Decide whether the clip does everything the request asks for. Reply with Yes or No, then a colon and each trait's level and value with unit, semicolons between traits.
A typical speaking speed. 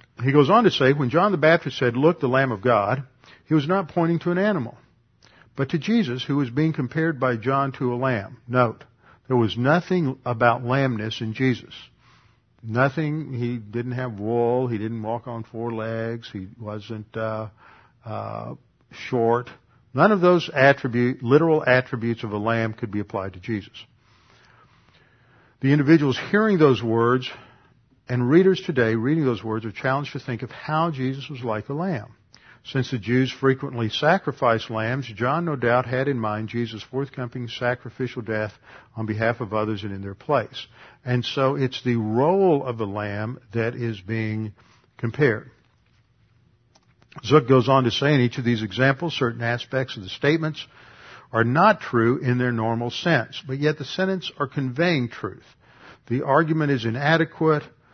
Yes: average, 170 wpm